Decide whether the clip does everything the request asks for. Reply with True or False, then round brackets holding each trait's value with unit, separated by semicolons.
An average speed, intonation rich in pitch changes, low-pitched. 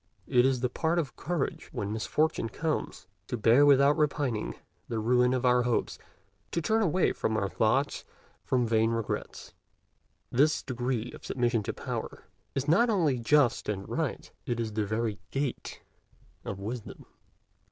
False (150 wpm; 4.3 semitones; 125 Hz)